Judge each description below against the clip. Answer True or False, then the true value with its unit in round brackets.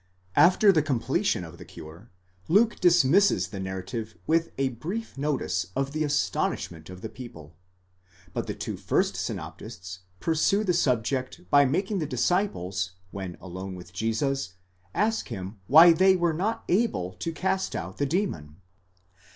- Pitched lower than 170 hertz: True (135 Hz)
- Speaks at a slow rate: False (150 wpm)